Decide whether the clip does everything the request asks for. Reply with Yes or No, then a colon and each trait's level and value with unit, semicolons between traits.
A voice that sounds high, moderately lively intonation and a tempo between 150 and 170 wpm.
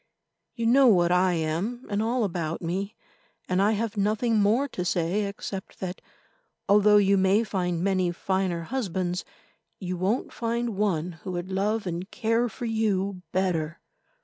Yes: high, 195 Hz; average, 3.4 semitones; average, 155 wpm